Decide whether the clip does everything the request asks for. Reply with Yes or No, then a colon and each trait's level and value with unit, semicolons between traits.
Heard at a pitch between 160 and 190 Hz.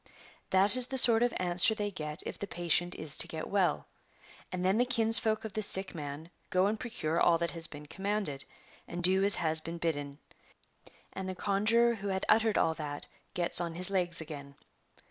Yes: medium, 185 Hz